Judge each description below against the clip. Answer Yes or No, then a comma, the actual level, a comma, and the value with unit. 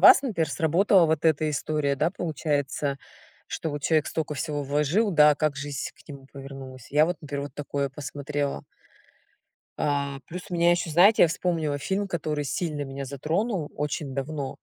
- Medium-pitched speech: Yes, medium, 150 Hz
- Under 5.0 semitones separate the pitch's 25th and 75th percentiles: Yes, average, 2.7 semitones